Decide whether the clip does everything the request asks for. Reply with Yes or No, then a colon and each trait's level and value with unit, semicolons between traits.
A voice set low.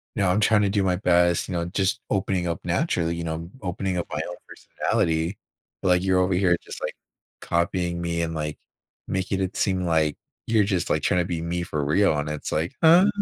Yes: very low, 90 Hz